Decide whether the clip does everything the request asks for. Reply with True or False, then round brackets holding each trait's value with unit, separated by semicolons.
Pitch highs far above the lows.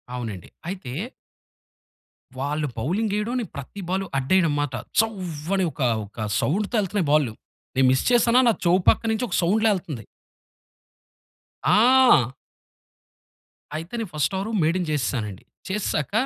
True (7.3 semitones)